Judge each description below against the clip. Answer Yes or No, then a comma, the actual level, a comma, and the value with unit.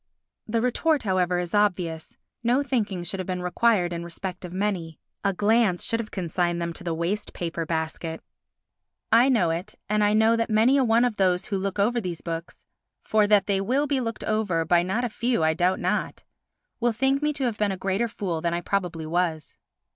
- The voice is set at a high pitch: Yes, high, 195 Hz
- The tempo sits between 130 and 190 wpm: No, average, 200 wpm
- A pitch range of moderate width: Yes, average, 4.7 semitones